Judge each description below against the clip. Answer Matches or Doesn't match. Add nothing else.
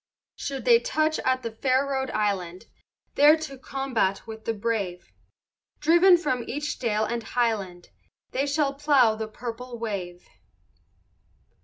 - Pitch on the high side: Matches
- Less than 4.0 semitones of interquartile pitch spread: Doesn't match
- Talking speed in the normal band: Doesn't match